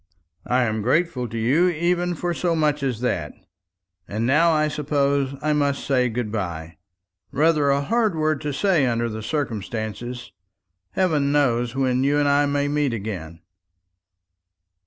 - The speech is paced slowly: No, average, 155 wpm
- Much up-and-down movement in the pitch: No, average, 4.5 semitones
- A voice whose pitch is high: No, medium, 140 Hz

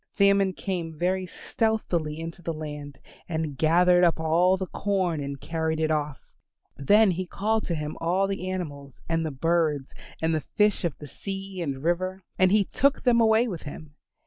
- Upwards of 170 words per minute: Yes, average, 180 wpm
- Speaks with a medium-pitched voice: Yes, medium, 170 Hz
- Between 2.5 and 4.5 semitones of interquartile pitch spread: Yes, average, 3.5 semitones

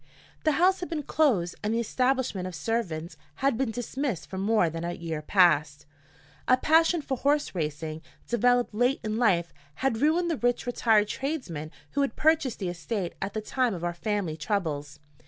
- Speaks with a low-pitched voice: No, high, 220 Hz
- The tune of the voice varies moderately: No, wide, 7.6 semitones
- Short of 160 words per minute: No, average, 180 wpm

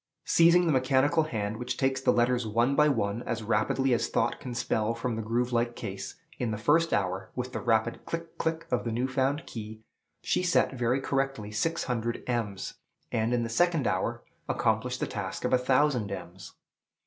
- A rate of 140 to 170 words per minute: No, average, 195 wpm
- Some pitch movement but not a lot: Yes, average, 3.5 semitones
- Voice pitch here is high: No, low, 120 Hz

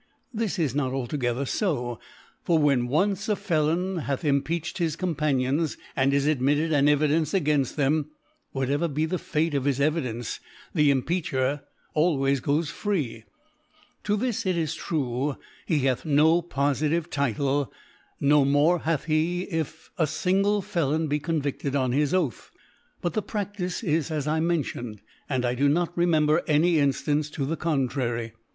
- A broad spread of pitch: No, average, 3.4 semitones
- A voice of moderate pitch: Yes, medium, 150 Hz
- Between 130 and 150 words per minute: No, average, 160 wpm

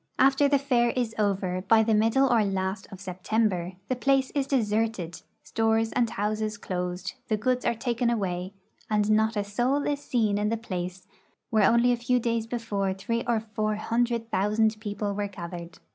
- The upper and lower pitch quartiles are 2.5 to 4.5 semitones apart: Yes, average, 3.1 semitones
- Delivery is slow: No, average, 180 wpm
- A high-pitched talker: Yes, high, 220 Hz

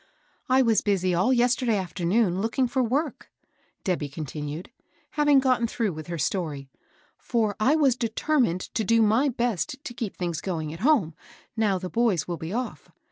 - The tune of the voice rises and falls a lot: Yes, wide, 6.0 semitones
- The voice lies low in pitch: No, high, 215 Hz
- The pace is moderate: Yes, average, 175 wpm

